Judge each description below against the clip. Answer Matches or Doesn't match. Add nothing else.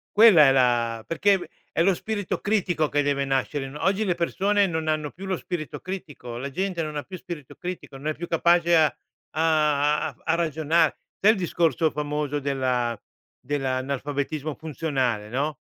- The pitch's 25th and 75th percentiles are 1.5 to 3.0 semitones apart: Doesn't match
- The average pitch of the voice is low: Doesn't match